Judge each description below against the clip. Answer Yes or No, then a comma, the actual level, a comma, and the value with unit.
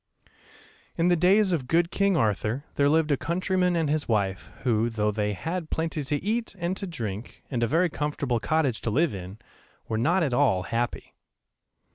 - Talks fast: No, average, 185 wpm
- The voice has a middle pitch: Yes, medium, 145 Hz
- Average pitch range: No, wide, 7.2 semitones